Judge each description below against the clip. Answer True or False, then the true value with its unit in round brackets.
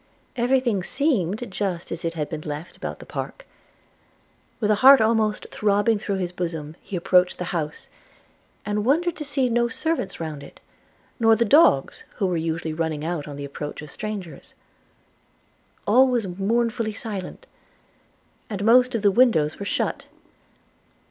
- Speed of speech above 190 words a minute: False (160 wpm)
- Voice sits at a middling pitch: False (205 Hz)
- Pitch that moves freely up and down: True (6.2 semitones)